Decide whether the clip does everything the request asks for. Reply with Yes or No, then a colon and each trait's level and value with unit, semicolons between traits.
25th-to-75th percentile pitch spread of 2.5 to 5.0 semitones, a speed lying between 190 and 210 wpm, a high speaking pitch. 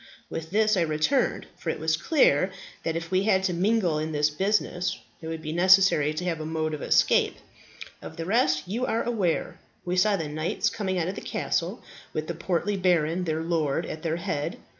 No: average, 3.3 semitones; fast, 205 wpm; medium, 170 Hz